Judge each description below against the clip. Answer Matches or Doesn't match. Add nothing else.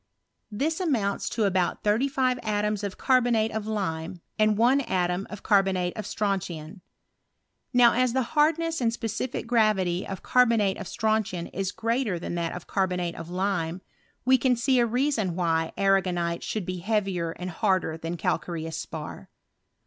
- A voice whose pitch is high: Matches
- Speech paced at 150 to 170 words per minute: Matches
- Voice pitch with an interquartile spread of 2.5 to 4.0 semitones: Doesn't match